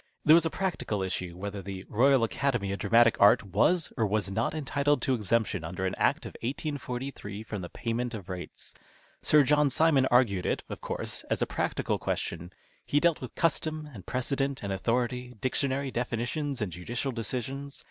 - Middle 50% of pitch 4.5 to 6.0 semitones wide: Yes, wide, 5.5 semitones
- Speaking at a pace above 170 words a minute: Yes, average, 180 wpm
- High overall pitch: No, low, 120 Hz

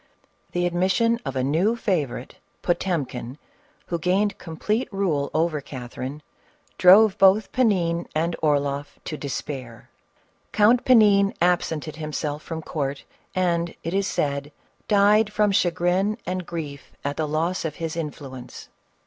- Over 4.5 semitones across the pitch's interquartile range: Yes, average, 4.9 semitones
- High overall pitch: No, medium, 170 Hz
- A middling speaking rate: No, slow, 130 wpm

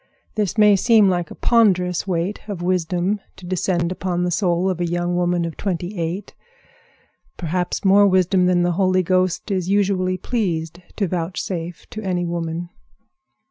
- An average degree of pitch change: No, narrow, 2.0 semitones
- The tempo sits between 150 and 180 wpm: Yes, average, 155 wpm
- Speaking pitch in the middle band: Yes, medium, 180 Hz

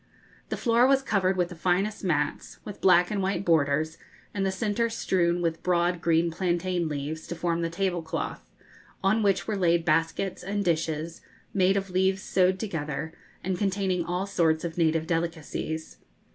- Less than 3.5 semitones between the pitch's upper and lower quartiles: Yes, average, 2.8 semitones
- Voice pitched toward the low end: No, medium, 175 Hz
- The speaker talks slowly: No, average, 165 wpm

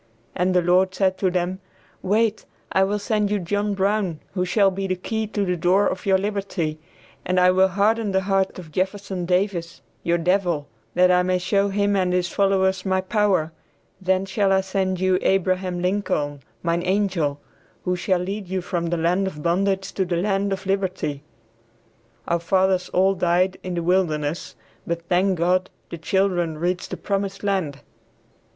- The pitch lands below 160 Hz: No, medium, 185 Hz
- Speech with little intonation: Yes, narrow, 1.8 semitones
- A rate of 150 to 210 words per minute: Yes, average, 175 wpm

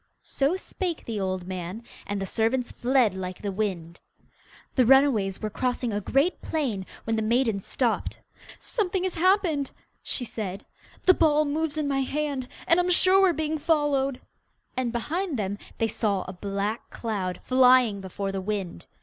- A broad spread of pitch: Yes, wide, 7.0 semitones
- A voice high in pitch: Yes, high, 245 Hz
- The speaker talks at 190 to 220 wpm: No, average, 165 wpm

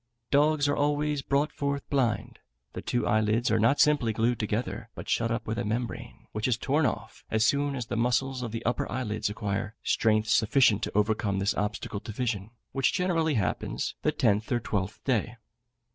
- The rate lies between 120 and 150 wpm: No, average, 190 wpm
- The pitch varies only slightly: No, average, 4.2 semitones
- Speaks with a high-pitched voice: No, low, 115 Hz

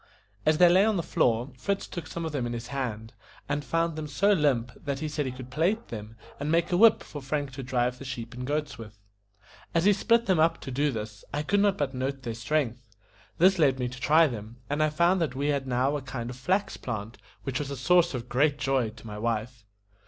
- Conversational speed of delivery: No, fast, 245 wpm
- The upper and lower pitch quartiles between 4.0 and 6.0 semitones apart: Yes, average, 4.5 semitones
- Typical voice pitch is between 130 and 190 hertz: Yes, medium, 140 Hz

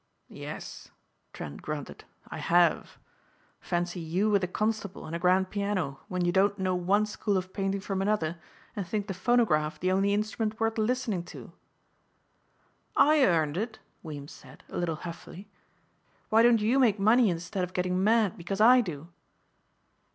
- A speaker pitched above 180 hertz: Yes, high, 190 Hz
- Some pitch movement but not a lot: Yes, average, 3.6 semitones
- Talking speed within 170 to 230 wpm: No, average, 160 wpm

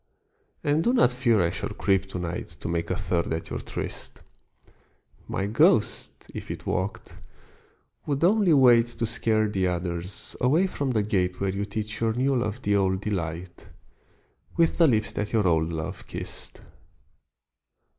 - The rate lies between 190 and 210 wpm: No, average, 165 wpm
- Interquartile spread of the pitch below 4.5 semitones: No, wide, 5.4 semitones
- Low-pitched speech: Yes, low, 105 Hz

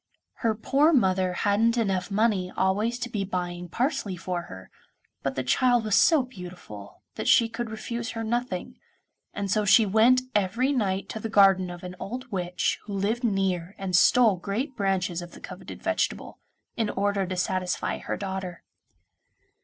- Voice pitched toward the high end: Yes, high, 200 Hz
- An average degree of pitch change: Yes, average, 4.0 semitones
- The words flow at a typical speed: Yes, average, 170 wpm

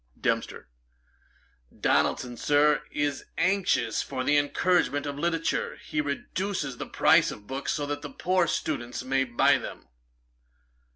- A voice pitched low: No, medium, 145 Hz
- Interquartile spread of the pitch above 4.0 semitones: No, average, 3.7 semitones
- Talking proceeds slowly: Yes, slow, 125 wpm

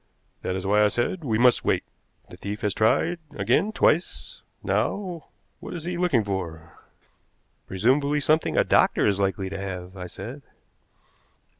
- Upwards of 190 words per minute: No, average, 155 wpm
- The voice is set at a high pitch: No, low, 110 Hz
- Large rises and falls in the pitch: Yes, wide, 8.2 semitones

